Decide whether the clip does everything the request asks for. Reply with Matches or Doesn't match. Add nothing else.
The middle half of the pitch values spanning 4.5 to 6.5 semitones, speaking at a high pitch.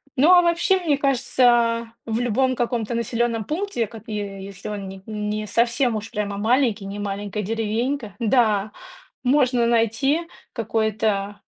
Doesn't match